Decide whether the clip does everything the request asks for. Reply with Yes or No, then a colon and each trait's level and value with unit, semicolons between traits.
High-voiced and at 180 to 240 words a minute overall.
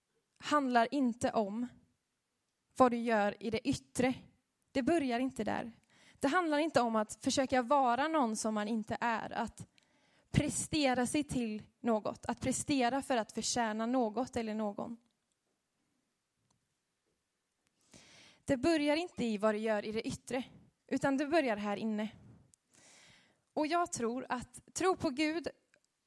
No: high, 245 Hz; average, 140 wpm